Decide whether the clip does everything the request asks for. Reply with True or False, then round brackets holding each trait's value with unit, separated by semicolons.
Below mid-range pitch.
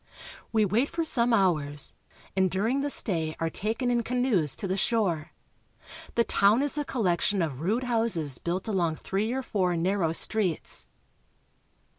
False (200 Hz)